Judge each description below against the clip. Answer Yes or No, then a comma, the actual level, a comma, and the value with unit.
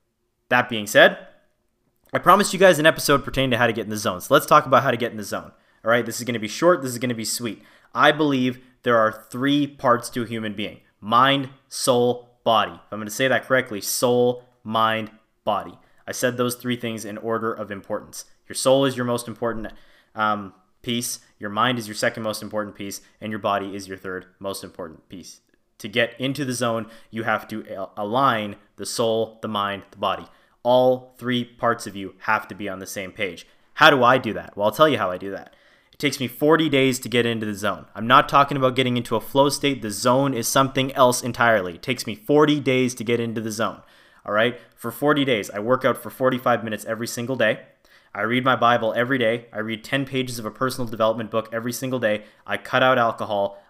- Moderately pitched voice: No, low, 115 Hz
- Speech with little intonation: No, average, 3.1 semitones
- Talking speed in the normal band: No, fast, 235 wpm